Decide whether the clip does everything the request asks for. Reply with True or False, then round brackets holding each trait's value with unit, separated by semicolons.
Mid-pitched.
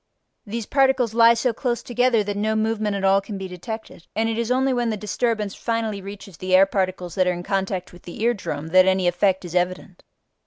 False (205 Hz)